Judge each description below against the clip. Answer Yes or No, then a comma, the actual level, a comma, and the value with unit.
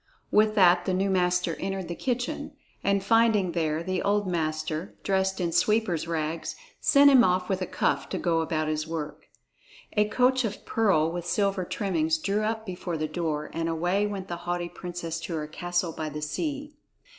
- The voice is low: No, medium, 180 Hz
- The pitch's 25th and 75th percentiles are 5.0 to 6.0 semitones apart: No, average, 3.8 semitones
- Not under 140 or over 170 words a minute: No, average, 185 wpm